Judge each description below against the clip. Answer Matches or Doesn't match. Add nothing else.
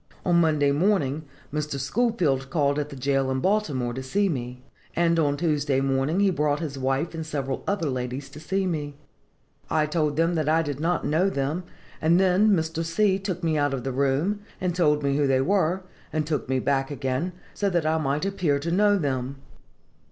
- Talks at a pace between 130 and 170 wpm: Doesn't match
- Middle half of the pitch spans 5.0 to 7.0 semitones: Doesn't match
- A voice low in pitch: Doesn't match